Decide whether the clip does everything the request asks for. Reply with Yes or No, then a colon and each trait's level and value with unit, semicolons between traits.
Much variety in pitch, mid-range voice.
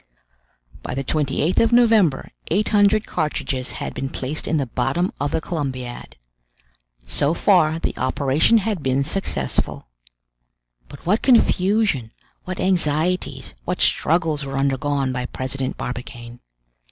Yes: wide, 5.7 semitones; medium, 150 Hz